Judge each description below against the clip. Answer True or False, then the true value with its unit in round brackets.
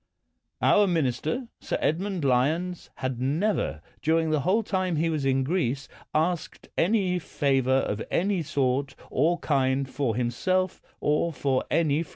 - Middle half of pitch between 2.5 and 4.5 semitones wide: False (5.1 semitones)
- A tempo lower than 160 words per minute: True (145 wpm)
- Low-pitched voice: False (155 Hz)